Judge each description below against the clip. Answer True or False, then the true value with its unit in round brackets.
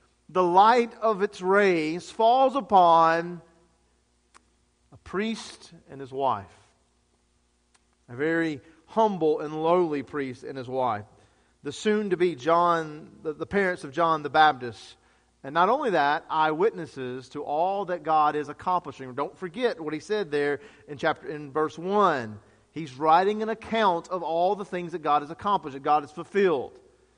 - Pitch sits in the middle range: True (160 Hz)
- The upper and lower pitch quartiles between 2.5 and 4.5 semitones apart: False (5.1 semitones)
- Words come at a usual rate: True (155 wpm)